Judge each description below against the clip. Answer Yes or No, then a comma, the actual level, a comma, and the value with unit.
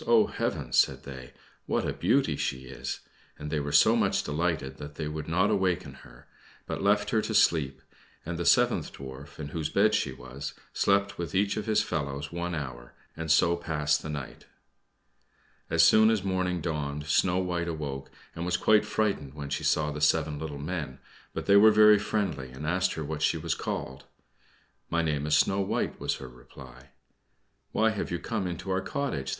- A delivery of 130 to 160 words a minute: No, average, 190 wpm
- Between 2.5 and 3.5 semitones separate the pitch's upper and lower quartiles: No, average, 4.7 semitones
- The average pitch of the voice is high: No, very low, 80 Hz